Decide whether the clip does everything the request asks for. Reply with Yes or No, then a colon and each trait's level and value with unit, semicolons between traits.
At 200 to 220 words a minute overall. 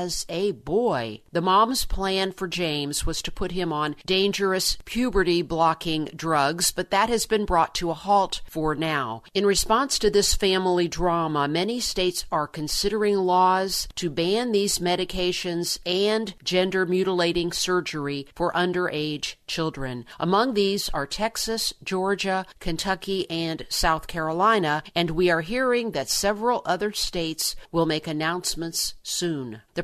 No: average, 140 wpm